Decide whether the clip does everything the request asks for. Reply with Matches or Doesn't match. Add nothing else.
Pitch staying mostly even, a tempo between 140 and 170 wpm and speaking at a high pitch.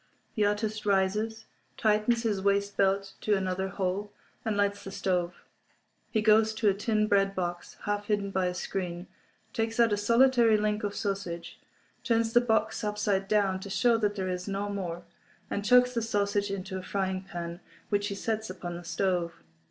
Doesn't match